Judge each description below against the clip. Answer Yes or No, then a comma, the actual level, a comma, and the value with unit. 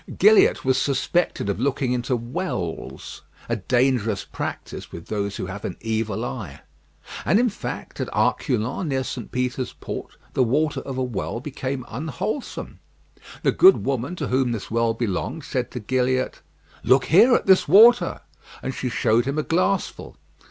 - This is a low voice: Yes, low, 130 Hz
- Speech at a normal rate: Yes, average, 160 wpm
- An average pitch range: Yes, average, 4.9 semitones